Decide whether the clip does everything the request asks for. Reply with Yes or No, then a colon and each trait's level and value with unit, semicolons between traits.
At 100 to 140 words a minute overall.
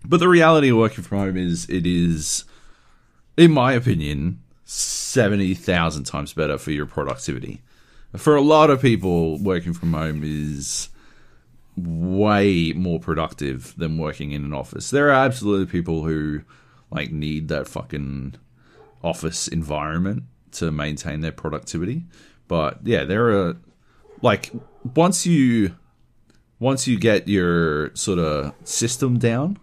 Yes: slow, 135 wpm